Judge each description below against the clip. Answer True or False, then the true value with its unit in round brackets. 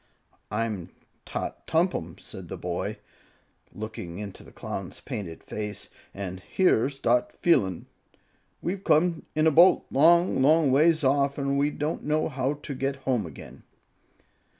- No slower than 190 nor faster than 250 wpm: False (145 wpm)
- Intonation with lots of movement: True (6.6 semitones)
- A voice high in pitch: False (135 Hz)